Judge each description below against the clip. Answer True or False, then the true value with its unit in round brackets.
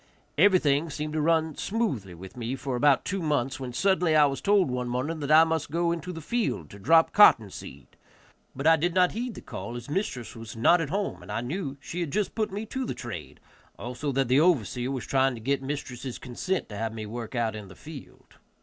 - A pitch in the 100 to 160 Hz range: True (140 Hz)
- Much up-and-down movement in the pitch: True (5.8 semitones)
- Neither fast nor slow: False (230 wpm)